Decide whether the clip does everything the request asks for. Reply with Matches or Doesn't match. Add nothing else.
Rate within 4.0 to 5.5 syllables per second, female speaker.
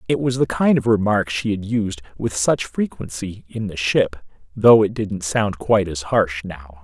Doesn't match